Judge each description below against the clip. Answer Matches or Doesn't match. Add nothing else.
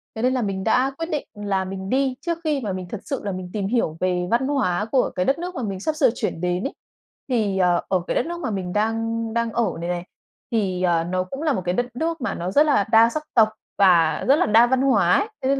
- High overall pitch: Matches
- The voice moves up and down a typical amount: Doesn't match